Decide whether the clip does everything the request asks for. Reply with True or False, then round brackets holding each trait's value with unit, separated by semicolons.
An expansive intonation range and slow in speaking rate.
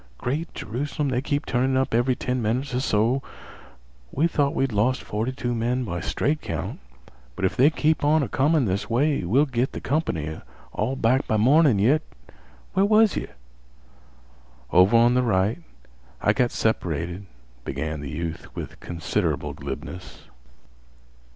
False (5.9 semitones; 150 wpm)